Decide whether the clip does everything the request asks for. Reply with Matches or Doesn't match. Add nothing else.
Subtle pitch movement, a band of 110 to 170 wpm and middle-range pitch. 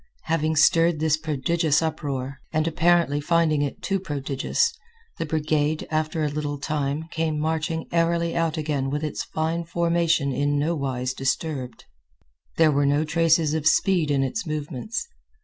Matches